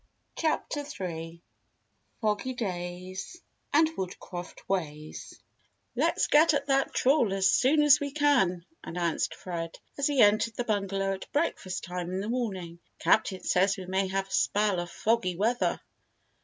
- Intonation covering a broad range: Yes, wide, 5.9 semitones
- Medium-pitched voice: No, high, 195 Hz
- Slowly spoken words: No, average, 145 wpm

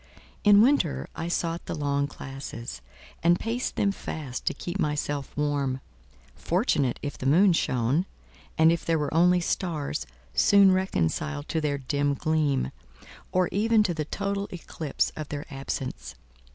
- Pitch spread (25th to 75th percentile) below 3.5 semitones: No, average, 4.7 semitones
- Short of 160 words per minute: Yes, average, 145 wpm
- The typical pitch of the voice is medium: Yes, medium, 155 Hz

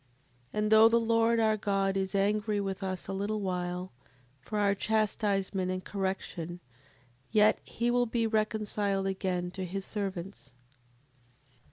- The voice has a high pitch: Yes, high, 200 Hz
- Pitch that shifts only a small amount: Yes, narrow, 2.2 semitones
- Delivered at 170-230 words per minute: No, average, 145 wpm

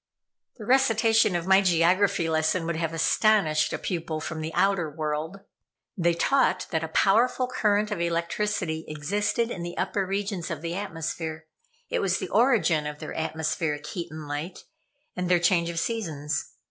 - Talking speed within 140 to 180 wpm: Yes, average, 165 wpm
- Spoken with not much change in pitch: No, average, 4.1 semitones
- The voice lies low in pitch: No, medium, 170 Hz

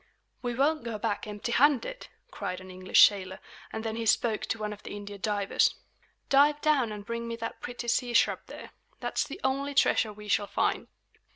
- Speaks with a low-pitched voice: No, high, 230 Hz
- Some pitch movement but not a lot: Yes, average, 4.2 semitones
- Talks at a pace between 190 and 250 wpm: Yes, average, 195 wpm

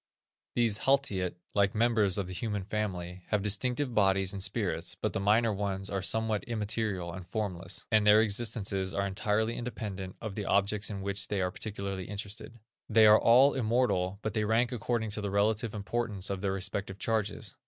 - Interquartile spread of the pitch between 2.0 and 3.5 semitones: Yes, narrow, 2.4 semitones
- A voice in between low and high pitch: No, low, 105 Hz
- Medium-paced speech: Yes, average, 180 wpm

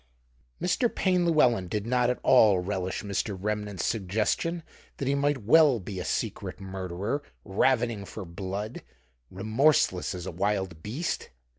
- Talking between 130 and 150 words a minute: Yes, average, 140 wpm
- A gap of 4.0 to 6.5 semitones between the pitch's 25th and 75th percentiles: Yes, wide, 5.5 semitones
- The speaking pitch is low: Yes, low, 105 Hz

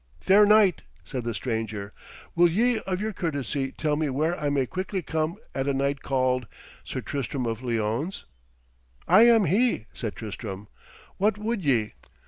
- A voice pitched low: No, medium, 145 Hz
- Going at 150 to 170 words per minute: Yes, average, 160 wpm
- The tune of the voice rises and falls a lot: Yes, wide, 7.5 semitones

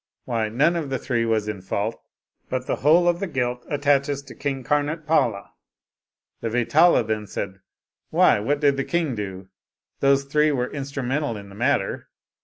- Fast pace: No, average, 175 wpm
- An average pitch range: Yes, average, 4.5 semitones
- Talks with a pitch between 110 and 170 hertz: Yes, low, 135 Hz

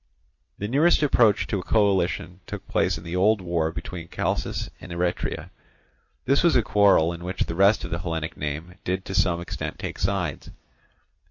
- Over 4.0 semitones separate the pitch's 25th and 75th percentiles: No, average, 3.2 semitones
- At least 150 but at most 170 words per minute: No, average, 180 wpm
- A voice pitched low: Yes, very low, 90 Hz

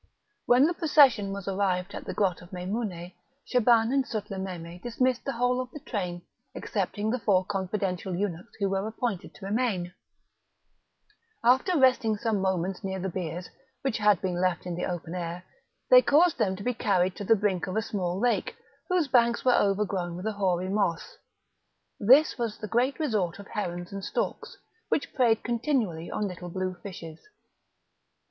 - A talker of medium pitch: No, high, 200 Hz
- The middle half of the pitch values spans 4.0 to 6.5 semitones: Yes, average, 4.6 semitones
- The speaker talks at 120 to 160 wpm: No, average, 170 wpm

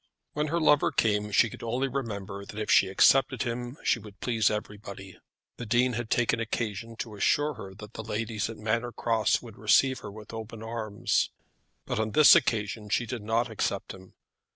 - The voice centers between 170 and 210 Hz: No, low, 110 Hz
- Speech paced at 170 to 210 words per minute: Yes, average, 190 wpm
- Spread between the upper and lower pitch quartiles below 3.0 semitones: Yes, narrow, 2.5 semitones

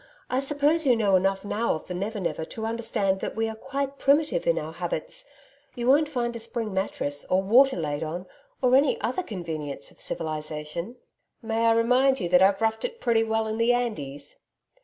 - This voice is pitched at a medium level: No, high, 225 Hz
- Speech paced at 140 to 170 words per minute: No, average, 200 wpm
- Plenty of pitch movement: Yes, wide, 5.7 semitones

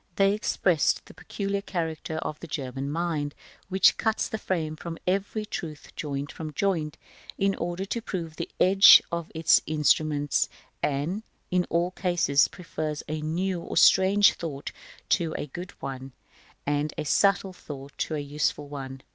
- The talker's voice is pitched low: No, medium, 165 Hz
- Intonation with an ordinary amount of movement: Yes, average, 4.2 semitones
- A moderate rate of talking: Yes, average, 160 wpm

